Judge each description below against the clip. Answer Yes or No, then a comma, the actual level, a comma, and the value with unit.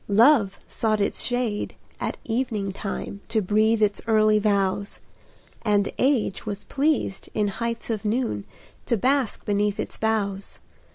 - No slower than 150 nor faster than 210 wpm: No, slow, 135 wpm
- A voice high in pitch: Yes, high, 215 Hz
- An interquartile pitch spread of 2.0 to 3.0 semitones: Yes, narrow, 2.4 semitones